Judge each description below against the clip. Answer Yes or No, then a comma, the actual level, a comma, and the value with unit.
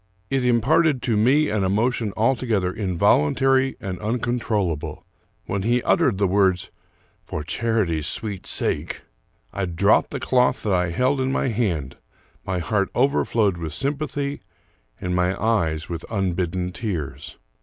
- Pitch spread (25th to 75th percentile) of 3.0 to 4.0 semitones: No, wide, 5.5 semitones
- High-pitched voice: No, low, 105 Hz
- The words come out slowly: No, average, 145 wpm